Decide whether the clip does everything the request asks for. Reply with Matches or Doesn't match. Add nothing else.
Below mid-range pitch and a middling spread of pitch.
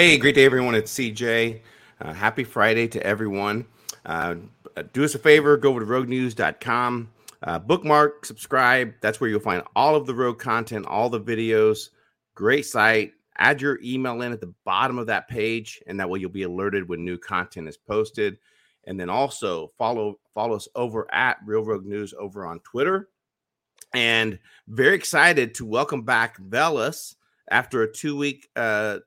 Matches